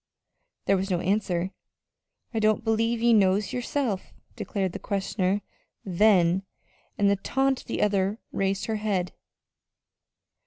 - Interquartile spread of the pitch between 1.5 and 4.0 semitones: Yes, narrow, 2.6 semitones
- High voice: Yes, high, 200 Hz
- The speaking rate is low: Yes, slow, 130 wpm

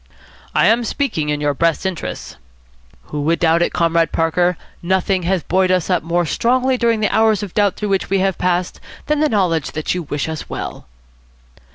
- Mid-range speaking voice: Yes, medium, 180 Hz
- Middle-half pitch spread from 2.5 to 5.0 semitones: Yes, average, 3.9 semitones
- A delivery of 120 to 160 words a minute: No, average, 195 wpm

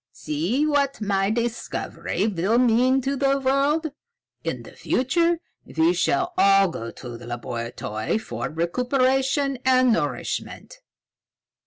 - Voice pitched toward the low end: No, high, 245 Hz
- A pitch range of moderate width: No, wide, 7.9 semitones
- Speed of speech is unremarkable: No, slow, 120 wpm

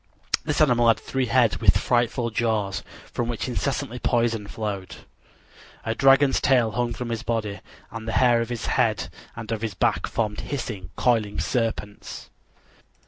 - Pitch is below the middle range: Yes, low, 115 Hz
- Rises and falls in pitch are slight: Yes, narrow, 2.1 semitones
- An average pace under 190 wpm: Yes, average, 155 wpm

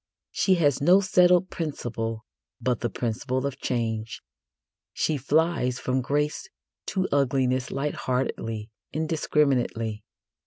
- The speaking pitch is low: Yes, low, 130 Hz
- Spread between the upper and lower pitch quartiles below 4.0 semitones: No, average, 4.3 semitones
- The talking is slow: Yes, slow, 105 wpm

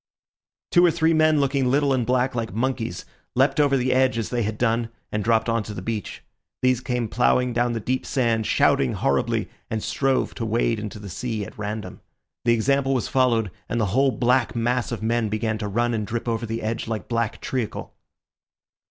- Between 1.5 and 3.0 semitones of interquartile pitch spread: Yes, average, 2.7 semitones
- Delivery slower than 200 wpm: No, fast, 205 wpm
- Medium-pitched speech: No, low, 120 Hz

